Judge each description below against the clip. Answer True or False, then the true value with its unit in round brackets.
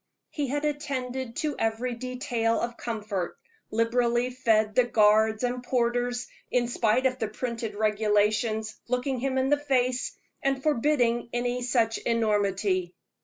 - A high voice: True (240 Hz)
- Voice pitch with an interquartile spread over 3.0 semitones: False (2.5 semitones)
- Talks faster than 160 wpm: False (135 wpm)